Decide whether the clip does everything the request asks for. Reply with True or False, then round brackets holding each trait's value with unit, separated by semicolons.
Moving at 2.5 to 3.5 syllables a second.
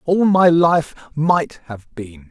True (3.2 syllables/s)